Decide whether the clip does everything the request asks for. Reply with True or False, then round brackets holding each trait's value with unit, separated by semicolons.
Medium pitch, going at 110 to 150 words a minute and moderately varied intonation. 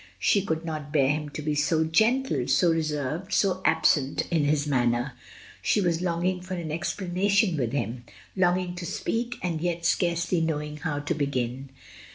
False (160 Hz; 175 wpm; 3.6 semitones)